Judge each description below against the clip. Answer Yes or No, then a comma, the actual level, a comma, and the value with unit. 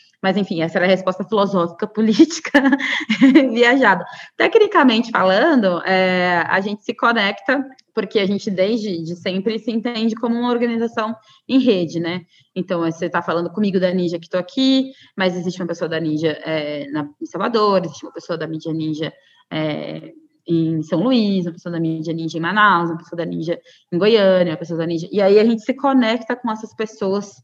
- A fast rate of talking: Yes, fast, 190 wpm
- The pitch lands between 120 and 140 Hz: No, high, 190 Hz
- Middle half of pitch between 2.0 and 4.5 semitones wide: No, average, 5.2 semitones